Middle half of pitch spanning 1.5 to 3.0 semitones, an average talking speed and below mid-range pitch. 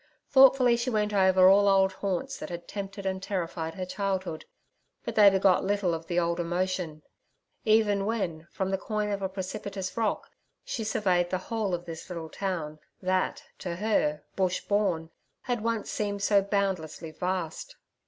No: narrow, 2.6 semitones; average, 160 wpm; high, 190 Hz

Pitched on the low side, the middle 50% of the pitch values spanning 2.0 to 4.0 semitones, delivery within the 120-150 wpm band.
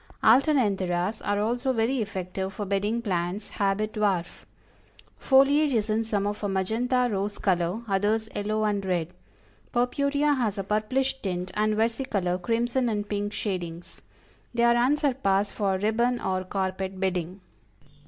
No: high, 210 Hz; average, 3.7 semitones; average, 140 wpm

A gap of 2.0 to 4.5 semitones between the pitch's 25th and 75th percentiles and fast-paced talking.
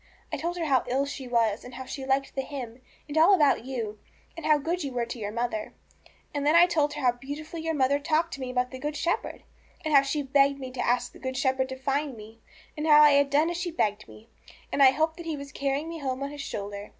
Yes: average, 3.2 semitones; fast, 265 wpm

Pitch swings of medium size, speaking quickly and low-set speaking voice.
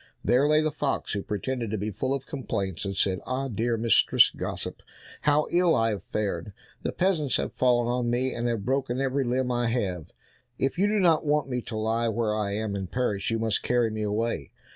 Yes: average, 3.9 semitones; fast, 215 wpm; low, 120 Hz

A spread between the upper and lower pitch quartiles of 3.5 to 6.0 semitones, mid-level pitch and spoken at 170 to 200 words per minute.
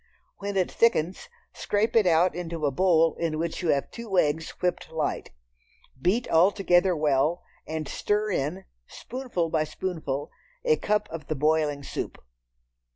No: average, 4.1 semitones; medium, 170 Hz; average, 155 wpm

